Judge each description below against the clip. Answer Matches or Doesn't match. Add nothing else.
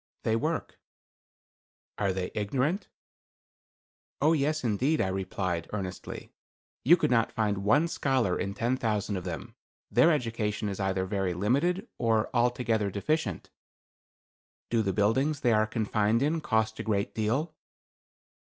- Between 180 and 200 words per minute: Doesn't match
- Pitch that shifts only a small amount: Doesn't match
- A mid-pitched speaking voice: Doesn't match